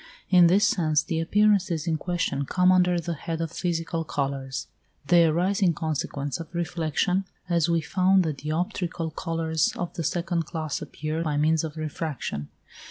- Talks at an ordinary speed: Yes, average, 165 wpm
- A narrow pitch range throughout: Yes, narrow, 2.2 semitones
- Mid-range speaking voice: Yes, medium, 165 Hz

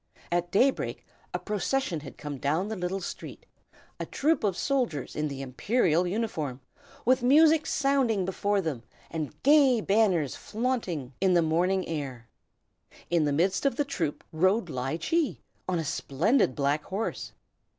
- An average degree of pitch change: No, wide, 7.4 semitones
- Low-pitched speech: No, medium, 185 Hz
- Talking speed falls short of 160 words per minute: Yes, average, 150 wpm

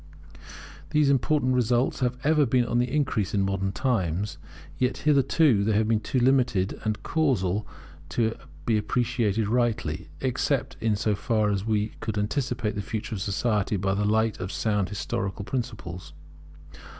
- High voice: No, low, 110 Hz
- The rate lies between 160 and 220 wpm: No, average, 150 wpm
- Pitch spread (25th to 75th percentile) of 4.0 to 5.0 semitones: No, average, 3.6 semitones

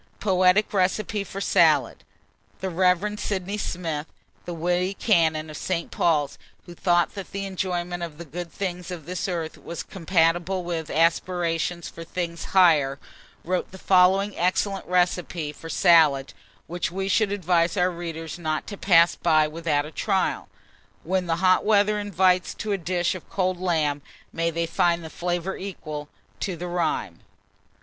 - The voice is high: No, medium, 175 Hz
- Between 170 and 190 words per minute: No, average, 155 wpm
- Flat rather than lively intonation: Yes, narrow, 2.2 semitones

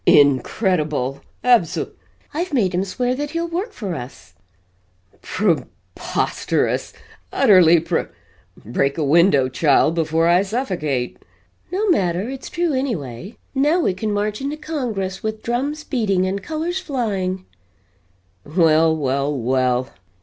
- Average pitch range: No, wide, 8.8 semitones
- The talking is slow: Yes, slow, 130 wpm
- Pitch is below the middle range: No, high, 190 Hz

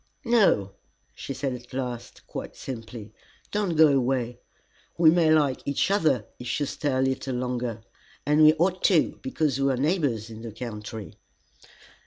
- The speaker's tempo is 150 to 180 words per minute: Yes, average, 160 wpm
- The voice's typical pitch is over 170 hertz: No, low, 135 Hz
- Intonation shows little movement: No, average, 4.4 semitones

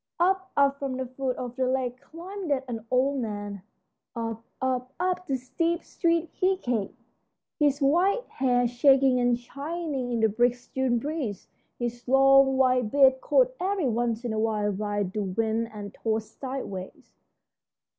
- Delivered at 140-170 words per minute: Yes, average, 155 wpm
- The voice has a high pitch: Yes, very high, 255 Hz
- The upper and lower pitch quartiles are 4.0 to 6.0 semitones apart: No, average, 3.6 semitones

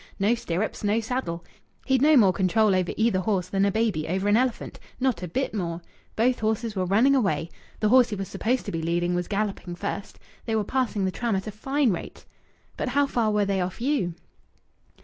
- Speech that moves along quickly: Yes, fast, 210 wpm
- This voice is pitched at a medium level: No, high, 210 Hz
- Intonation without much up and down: No, average, 4.3 semitones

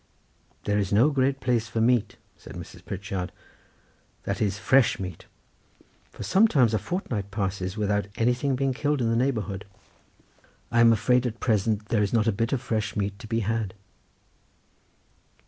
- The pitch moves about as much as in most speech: Yes, average, 3.4 semitones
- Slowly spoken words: No, average, 165 wpm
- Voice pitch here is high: No, low, 115 Hz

